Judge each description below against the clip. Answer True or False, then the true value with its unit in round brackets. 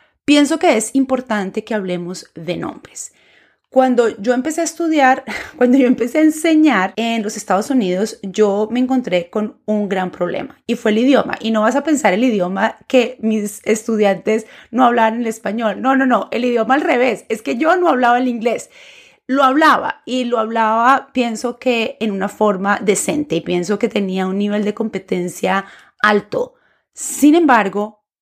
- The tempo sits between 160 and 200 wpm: True (175 wpm)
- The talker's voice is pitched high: True (230 Hz)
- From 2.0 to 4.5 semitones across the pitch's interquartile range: True (4.0 semitones)